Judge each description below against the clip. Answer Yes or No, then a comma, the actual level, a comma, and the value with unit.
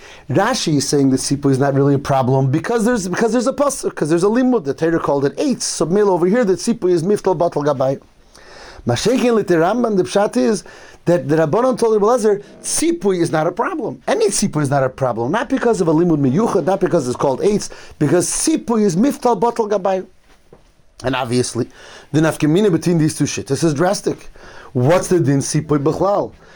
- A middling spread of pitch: No, wide, 6.9 semitones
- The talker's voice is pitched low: No, medium, 175 Hz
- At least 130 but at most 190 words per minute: No, fast, 205 wpm